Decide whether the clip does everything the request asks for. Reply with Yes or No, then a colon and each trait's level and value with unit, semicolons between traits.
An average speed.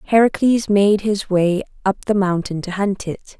Yes: average, 175 wpm